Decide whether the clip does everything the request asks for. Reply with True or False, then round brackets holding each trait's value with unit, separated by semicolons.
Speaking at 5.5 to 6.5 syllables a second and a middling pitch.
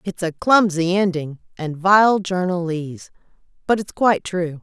False (4.5 syllables/s; 180 Hz)